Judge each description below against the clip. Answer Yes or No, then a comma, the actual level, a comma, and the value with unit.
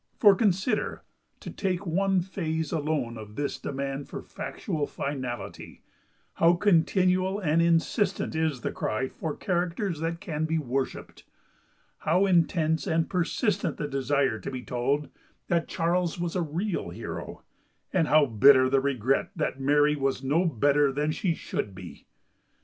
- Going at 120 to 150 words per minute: Yes, average, 140 wpm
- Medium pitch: Yes, medium, 155 Hz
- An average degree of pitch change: Yes, average, 4.2 semitones